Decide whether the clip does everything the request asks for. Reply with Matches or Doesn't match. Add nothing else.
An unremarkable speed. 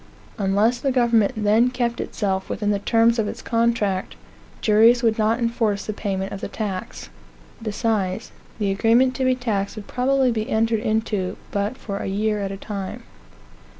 Matches